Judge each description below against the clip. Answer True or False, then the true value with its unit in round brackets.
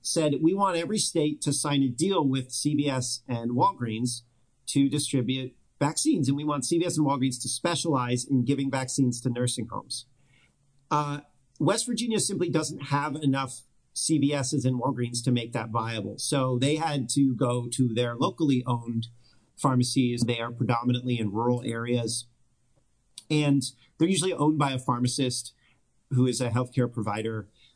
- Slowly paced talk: False (155 wpm)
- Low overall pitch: True (130 Hz)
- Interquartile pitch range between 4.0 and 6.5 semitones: False (3.0 semitones)